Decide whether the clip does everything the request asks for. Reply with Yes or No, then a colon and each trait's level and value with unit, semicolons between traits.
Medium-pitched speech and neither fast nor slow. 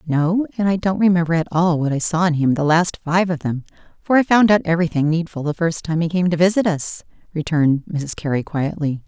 No: medium, 165 Hz; fast, 230 wpm